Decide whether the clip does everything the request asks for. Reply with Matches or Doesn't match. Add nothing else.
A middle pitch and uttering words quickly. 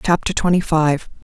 Doesn't match